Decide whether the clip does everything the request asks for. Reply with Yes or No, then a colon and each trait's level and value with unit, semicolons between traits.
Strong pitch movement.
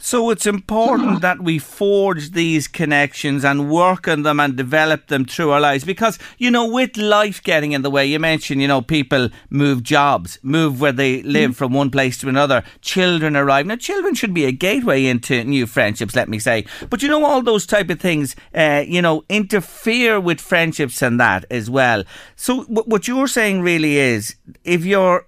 Yes: wide, 6.8 semitones